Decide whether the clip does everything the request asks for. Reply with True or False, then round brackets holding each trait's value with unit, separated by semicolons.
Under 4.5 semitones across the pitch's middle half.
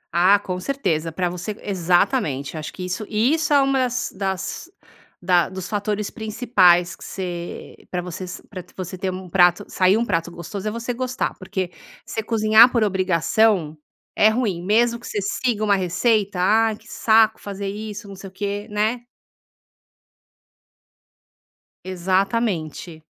True (3.4 semitones)